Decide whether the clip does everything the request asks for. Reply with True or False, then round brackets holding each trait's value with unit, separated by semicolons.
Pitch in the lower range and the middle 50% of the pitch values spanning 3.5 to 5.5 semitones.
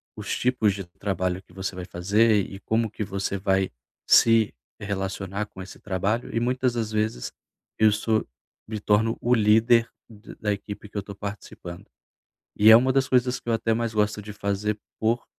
False (105 Hz; 2.4 semitones)